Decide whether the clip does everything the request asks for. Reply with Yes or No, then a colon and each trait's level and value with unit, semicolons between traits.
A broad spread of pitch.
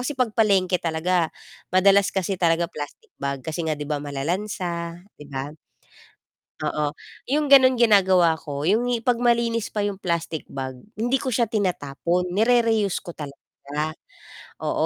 Yes: wide, 6.1 semitones